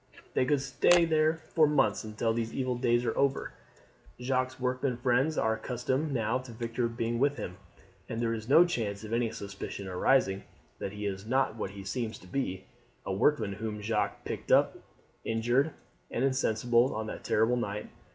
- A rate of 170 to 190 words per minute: Yes, average, 180 wpm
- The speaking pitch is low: Yes, low, 120 Hz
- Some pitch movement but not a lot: Yes, average, 3.4 semitones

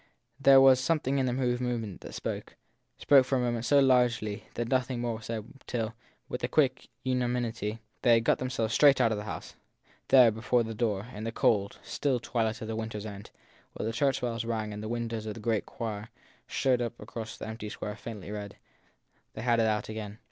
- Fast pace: Yes, fast, 215 wpm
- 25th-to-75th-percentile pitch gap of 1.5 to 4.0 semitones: Yes, narrow, 2.4 semitones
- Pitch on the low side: Yes, low, 115 Hz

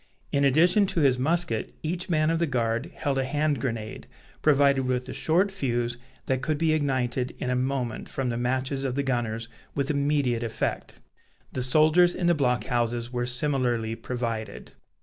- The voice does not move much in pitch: No, average, 3.9 semitones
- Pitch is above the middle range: No, low, 130 Hz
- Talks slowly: No, average, 175 wpm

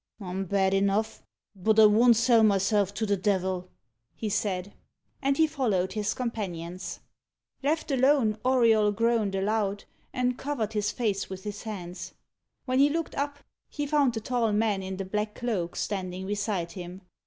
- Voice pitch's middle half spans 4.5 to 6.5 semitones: No, average, 3.7 semitones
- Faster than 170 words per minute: No, average, 160 wpm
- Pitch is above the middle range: Yes, high, 210 Hz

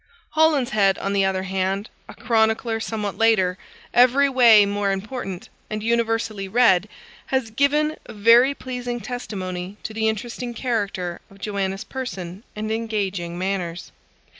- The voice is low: No, high, 215 Hz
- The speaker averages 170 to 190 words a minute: No, slow, 135 wpm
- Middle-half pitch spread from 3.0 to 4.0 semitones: Yes, average, 3.7 semitones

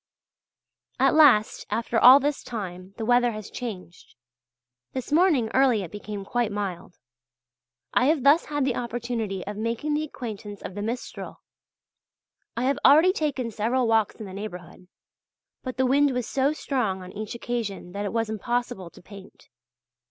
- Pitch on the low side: No, high, 230 Hz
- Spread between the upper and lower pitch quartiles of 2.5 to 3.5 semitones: No, average, 4.2 semitones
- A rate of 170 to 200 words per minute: No, average, 160 wpm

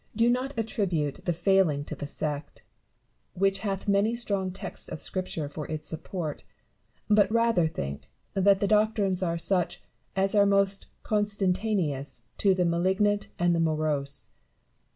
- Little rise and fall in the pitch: No, average, 4.3 semitones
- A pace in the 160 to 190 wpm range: No, average, 145 wpm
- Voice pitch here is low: No, high, 190 Hz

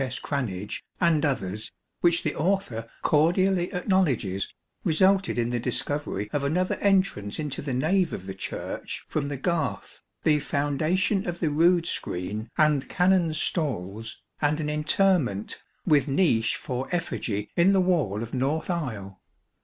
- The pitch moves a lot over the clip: Yes, wide, 7.0 semitones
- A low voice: No, medium, 150 Hz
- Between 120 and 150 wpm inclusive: Yes, average, 145 wpm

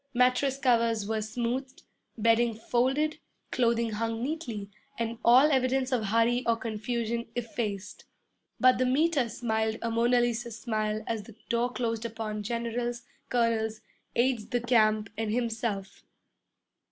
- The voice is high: Yes, high, 235 Hz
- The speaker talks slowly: Yes, slow, 130 wpm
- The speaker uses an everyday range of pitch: No, narrow, 2.0 semitones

